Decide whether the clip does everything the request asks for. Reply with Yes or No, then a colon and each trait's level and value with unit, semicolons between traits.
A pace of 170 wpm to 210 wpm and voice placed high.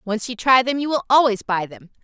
No: fast, 265 wpm; high, 235 Hz